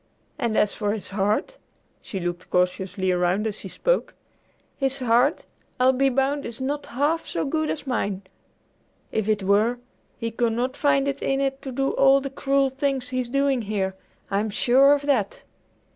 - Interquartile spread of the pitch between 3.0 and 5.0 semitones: Yes, average, 4.7 semitones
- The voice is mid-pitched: No, very high, 250 Hz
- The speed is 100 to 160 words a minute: No, average, 175 wpm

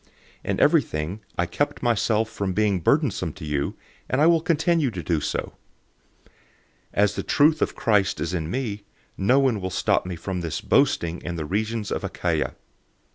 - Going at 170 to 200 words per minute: Yes, average, 180 wpm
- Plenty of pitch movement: Yes, wide, 6.4 semitones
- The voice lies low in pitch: Yes, low, 100 Hz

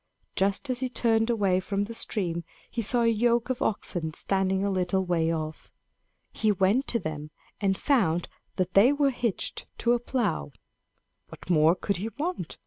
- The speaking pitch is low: No, high, 200 Hz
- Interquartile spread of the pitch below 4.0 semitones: No, average, 4.8 semitones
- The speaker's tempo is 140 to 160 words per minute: No, average, 175 wpm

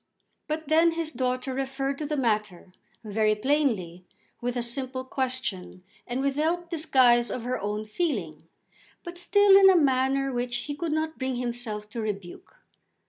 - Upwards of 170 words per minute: No, average, 155 wpm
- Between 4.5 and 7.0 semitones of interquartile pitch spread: Yes, wide, 5.4 semitones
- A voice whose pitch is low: No, very high, 260 Hz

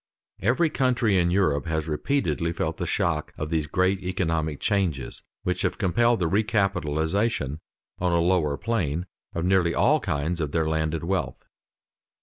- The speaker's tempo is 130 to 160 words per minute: Yes, average, 150 wpm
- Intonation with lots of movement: No, average, 3.8 semitones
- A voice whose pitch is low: Yes, very low, 85 Hz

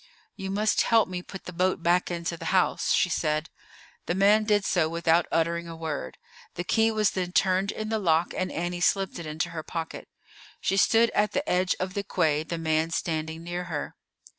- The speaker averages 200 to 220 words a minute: Yes, fast, 205 wpm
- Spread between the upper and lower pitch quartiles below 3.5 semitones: Yes, average, 2.8 semitones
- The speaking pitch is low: No, medium, 175 Hz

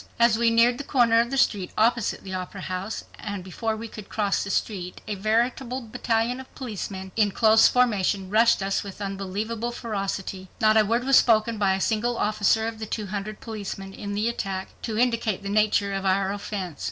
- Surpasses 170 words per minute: Yes, average, 200 wpm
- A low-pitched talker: No, high, 215 Hz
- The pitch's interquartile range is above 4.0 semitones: No, average, 2.8 semitones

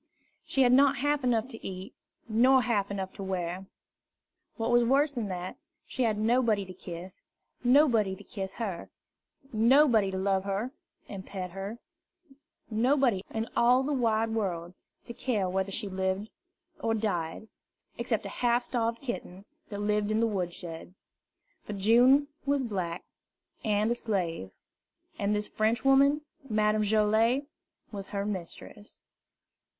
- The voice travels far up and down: No, average, 3.9 semitones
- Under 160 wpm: Yes, average, 145 wpm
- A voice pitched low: No, high, 215 Hz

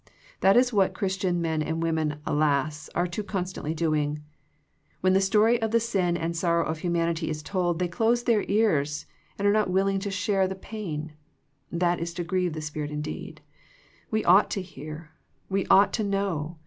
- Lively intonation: No, average, 3.8 semitones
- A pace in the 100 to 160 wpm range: No, average, 185 wpm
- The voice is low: No, medium, 175 Hz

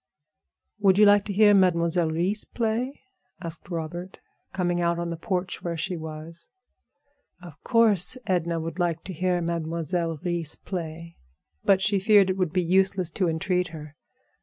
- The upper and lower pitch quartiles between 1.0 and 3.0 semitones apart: Yes, narrow, 2.4 semitones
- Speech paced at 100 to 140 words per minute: No, average, 160 wpm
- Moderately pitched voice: Yes, medium, 175 Hz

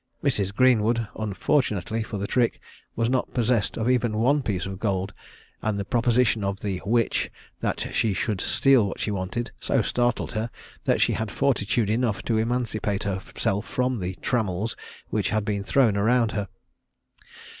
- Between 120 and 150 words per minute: No, average, 165 wpm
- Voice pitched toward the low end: Yes, low, 110 Hz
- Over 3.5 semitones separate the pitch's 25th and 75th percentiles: No, average, 3.2 semitones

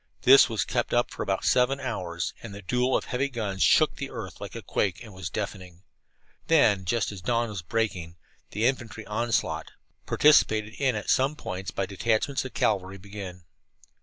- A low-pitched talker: Yes, low, 105 Hz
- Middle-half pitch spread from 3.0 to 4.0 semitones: No, average, 4.6 semitones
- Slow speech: No, average, 180 wpm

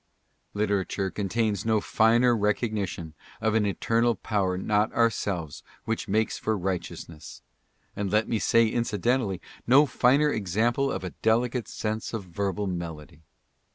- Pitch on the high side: No, low, 105 Hz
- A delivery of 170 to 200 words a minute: No, average, 145 wpm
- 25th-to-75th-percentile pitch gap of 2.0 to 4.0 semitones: Yes, average, 3.3 semitones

